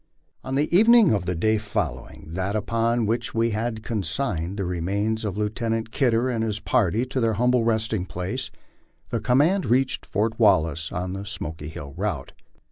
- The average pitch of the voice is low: Yes, low, 110 Hz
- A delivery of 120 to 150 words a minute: No, average, 170 wpm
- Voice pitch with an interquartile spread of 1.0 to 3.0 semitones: No, average, 4.0 semitones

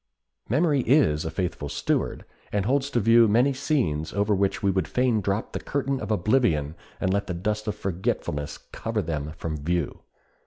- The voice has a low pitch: Yes, low, 100 Hz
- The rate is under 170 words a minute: No, average, 180 wpm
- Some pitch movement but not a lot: No, wide, 6.8 semitones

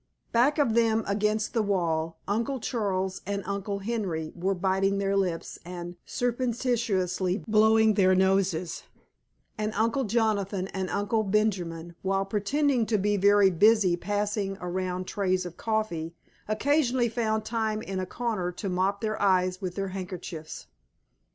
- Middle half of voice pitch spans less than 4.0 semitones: Yes, average, 2.9 semitones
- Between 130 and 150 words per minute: Yes, average, 140 wpm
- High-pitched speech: Yes, high, 200 Hz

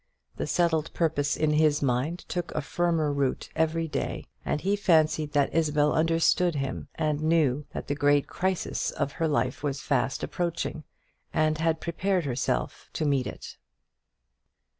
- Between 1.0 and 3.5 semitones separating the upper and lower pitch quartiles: Yes, narrow, 2.4 semitones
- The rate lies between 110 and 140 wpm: No, average, 155 wpm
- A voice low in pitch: No, medium, 155 Hz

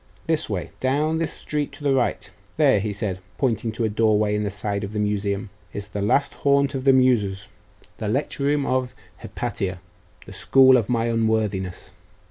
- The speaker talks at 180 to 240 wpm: Yes, average, 185 wpm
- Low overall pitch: Yes, low, 110 Hz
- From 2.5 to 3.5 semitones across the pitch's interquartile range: No, average, 4.5 semitones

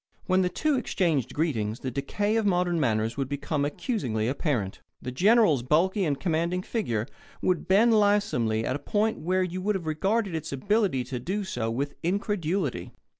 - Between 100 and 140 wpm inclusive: No, average, 175 wpm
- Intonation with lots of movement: Yes, wide, 7.3 semitones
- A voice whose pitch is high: No, medium, 170 Hz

